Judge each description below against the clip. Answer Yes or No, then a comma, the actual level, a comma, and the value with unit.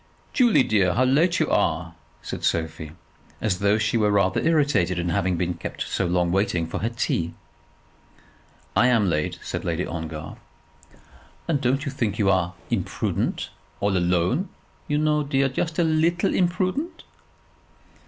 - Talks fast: No, average, 155 wpm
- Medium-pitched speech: No, low, 105 Hz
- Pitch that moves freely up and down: Yes, wide, 9.0 semitones